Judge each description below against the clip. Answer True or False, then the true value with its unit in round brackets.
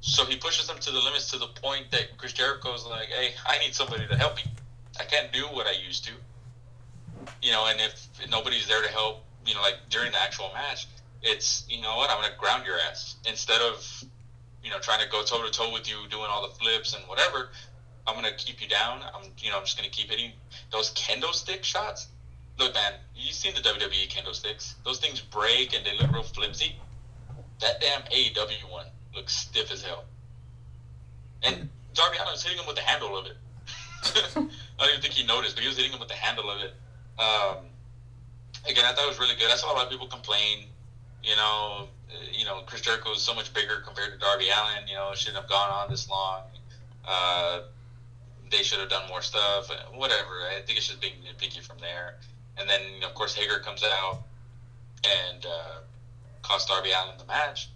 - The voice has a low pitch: True (120 Hz)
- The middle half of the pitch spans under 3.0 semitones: True (2.5 semitones)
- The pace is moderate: False (215 wpm)